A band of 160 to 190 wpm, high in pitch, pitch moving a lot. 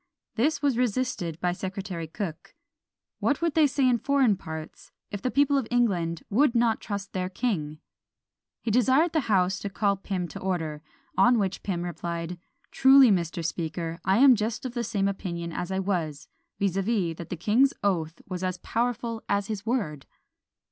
Yes: average, 170 wpm; high, 200 Hz; wide, 5.7 semitones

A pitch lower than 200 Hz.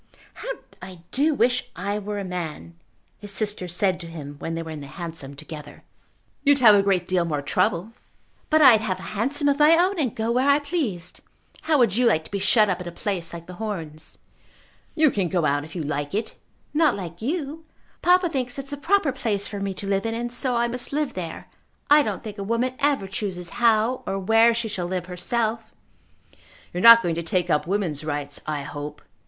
No: high, 205 Hz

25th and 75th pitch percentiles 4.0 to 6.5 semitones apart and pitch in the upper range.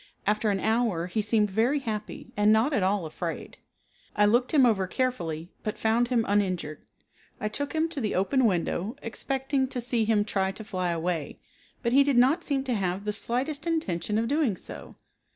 Yes: average, 4.9 semitones; high, 220 Hz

